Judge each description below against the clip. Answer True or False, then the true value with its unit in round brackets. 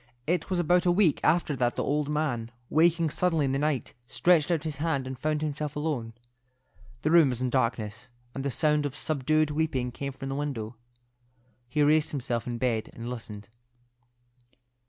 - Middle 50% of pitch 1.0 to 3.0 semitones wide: False (3.6 semitones)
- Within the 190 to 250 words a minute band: False (180 wpm)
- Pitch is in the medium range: True (145 Hz)